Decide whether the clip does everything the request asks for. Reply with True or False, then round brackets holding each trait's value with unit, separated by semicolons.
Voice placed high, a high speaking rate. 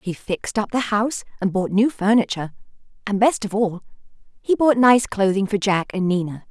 False (210 Hz; 195 wpm)